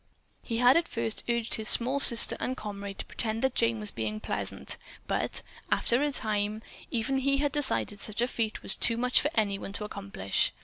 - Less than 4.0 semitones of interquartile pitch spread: Yes, average, 3.6 semitones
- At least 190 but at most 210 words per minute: Yes, fast, 205 wpm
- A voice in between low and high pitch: No, high, 225 Hz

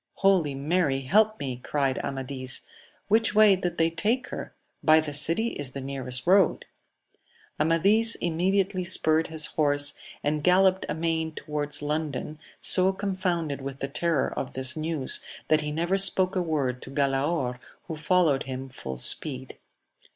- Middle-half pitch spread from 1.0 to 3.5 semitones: No, average, 4.9 semitones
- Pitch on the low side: No, medium, 155 Hz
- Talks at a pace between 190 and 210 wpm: No, average, 150 wpm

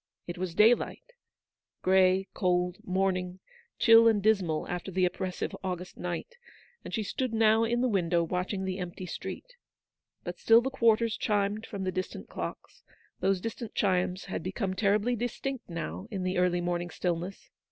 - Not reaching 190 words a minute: Yes, average, 160 wpm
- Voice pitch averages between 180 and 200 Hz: Yes, high, 190 Hz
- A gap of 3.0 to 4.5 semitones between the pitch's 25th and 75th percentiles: Yes, average, 3.5 semitones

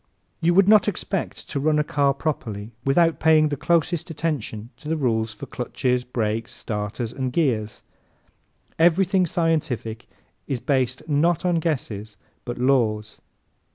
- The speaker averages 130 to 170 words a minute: Yes, average, 140 wpm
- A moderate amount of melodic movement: No, wide, 6.0 semitones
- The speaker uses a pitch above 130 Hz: Yes, medium, 140 Hz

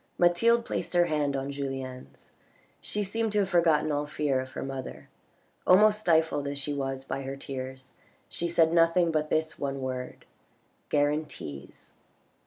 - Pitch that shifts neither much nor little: Yes, average, 4.1 semitones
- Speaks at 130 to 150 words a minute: No, average, 160 wpm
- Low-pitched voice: No, medium, 145 Hz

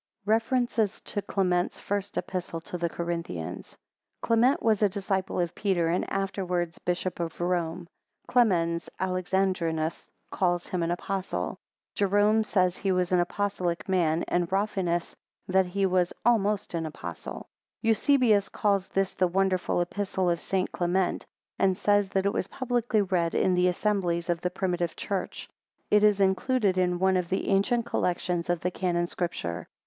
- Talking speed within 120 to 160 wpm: Yes, average, 155 wpm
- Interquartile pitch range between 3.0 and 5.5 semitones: No, narrow, 2.5 semitones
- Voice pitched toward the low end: No, medium, 185 Hz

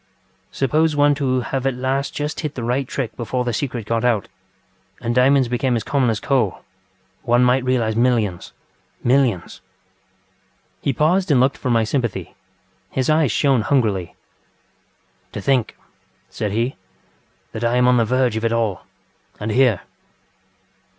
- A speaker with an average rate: Yes, average, 155 wpm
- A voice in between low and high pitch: No, low, 125 Hz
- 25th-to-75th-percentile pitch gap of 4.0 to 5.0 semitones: No, average, 2.7 semitones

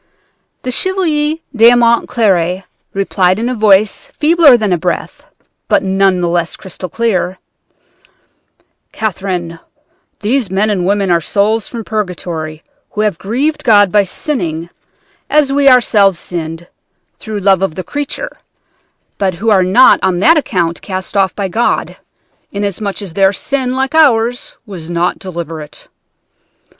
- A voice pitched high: Yes, high, 200 Hz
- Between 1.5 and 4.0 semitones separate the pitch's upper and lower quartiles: No, average, 4.7 semitones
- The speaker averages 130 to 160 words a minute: Yes, average, 140 wpm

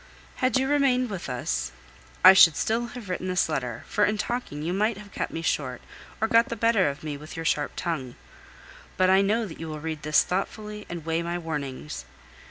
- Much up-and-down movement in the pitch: Yes, wide, 5.9 semitones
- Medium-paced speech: No, fast, 210 wpm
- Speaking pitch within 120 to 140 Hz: No, medium, 180 Hz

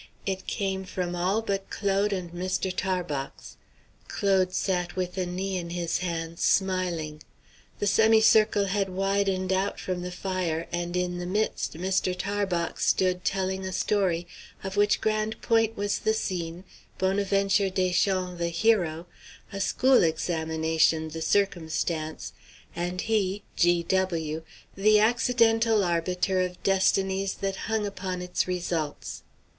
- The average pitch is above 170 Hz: Yes, medium, 185 Hz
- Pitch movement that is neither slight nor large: No, narrow, 2.2 semitones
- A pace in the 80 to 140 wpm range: Yes, slow, 135 wpm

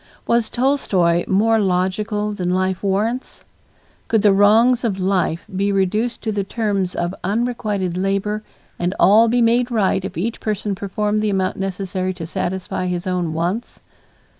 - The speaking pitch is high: Yes, high, 200 Hz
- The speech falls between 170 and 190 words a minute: No, average, 155 wpm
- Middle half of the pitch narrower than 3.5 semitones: Yes, average, 2.8 semitones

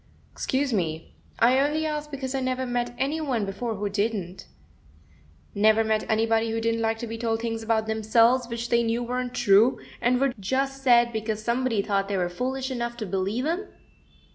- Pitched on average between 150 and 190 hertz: No, high, 235 Hz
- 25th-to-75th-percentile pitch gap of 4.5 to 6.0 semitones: No, average, 2.8 semitones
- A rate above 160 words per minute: Yes, average, 190 wpm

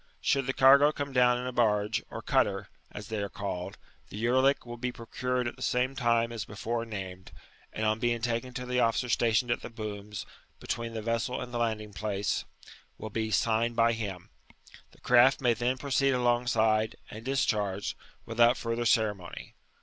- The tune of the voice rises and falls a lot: No, narrow, 2.4 semitones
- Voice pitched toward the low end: Yes, low, 115 Hz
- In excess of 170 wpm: Yes, average, 180 wpm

